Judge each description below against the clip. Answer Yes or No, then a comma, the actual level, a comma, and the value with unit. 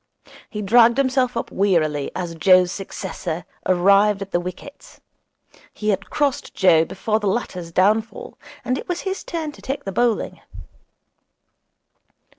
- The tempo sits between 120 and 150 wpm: Yes, average, 140 wpm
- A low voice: No, high, 200 Hz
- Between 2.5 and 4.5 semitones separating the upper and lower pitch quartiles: No, average, 4.9 semitones